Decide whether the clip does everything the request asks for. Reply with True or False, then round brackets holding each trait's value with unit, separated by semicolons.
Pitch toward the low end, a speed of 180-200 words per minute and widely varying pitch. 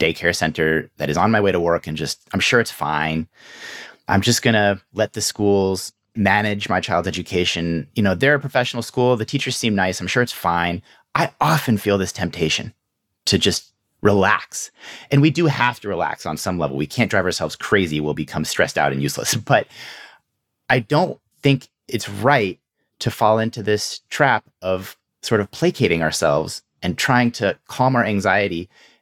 True (100 Hz; 185 wpm; 5.7 semitones)